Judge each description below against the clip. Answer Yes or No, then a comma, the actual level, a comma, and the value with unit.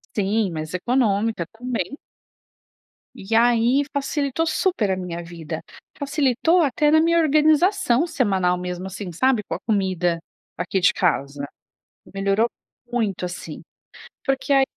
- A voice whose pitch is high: Yes, high, 225 Hz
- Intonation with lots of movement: Yes, wide, 7.3 semitones